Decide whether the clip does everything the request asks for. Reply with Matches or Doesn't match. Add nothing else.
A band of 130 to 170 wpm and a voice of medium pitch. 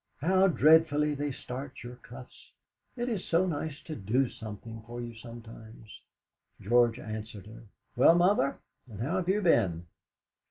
Doesn't match